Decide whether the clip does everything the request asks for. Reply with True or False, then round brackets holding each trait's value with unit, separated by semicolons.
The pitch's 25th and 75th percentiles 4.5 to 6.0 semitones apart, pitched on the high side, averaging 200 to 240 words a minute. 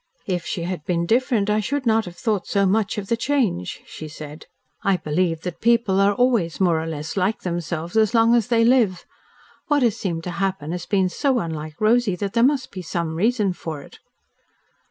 True (5.1 semitones; 195 Hz; 205 wpm)